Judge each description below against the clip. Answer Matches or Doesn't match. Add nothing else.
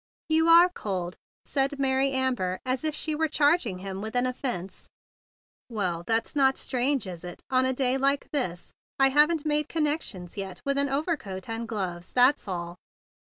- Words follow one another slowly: Doesn't match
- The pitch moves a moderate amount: Doesn't match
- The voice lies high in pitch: Matches